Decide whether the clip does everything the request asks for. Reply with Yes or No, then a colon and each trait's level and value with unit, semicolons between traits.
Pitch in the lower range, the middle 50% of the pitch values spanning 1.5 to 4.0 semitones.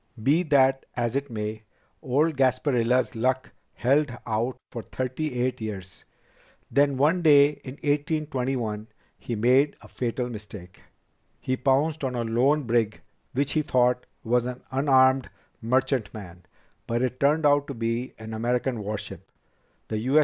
Yes: low, 130 Hz; average, 3.5 semitones